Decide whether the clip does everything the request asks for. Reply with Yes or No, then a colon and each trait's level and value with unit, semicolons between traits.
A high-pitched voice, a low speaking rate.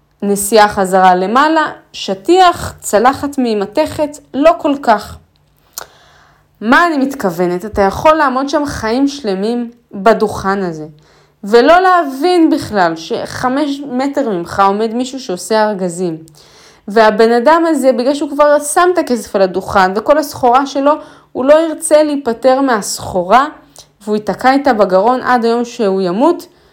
No: high, 245 Hz; average, 130 wpm